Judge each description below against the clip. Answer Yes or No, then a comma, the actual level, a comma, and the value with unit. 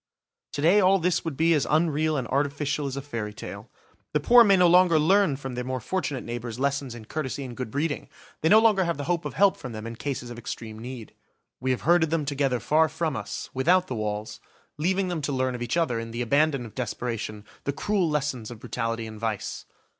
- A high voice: No, medium, 140 Hz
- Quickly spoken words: Yes, fast, 230 wpm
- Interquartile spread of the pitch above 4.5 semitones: Yes, average, 5.2 semitones